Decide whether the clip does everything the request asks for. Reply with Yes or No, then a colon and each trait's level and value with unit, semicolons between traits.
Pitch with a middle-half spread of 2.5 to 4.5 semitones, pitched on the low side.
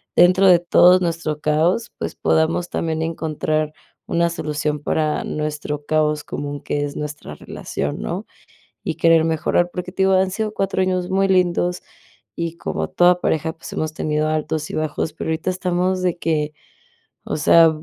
No: average, 2.8 semitones; medium, 160 Hz